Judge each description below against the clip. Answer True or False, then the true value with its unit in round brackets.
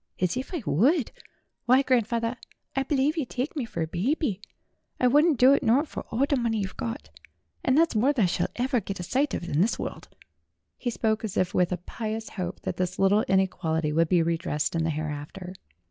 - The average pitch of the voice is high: True (220 Hz)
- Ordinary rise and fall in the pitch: False (6.6 semitones)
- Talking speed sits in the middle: False (215 wpm)